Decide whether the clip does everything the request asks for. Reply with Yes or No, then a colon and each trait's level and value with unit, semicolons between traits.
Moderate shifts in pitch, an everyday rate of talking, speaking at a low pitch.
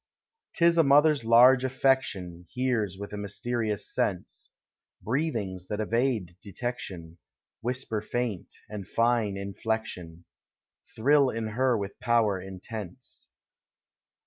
No: average, 4.4 semitones; slow, 115 wpm; low, 110 Hz